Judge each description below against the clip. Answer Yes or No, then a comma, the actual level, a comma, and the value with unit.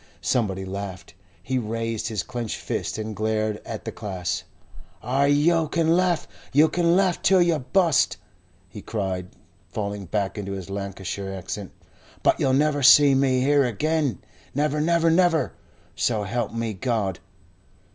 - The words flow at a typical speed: Yes, average, 145 wpm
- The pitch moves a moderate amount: No, wide, 7.0 semitones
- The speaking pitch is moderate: No, low, 120 Hz